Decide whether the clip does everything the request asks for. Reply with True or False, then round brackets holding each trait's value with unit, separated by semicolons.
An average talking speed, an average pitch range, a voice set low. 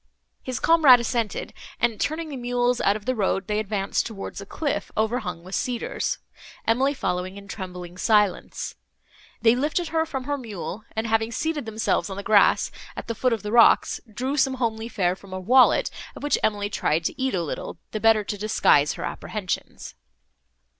False (185 wpm; 4.1 semitones; 220 Hz)